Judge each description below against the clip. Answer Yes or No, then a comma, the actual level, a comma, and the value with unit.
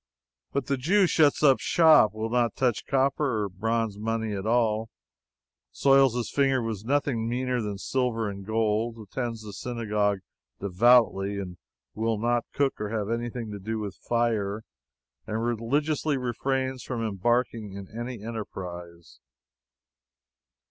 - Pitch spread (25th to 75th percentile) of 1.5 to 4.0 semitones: Yes, average, 3.1 semitones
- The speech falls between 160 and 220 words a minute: No, slow, 135 wpm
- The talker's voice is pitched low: Yes, low, 115 Hz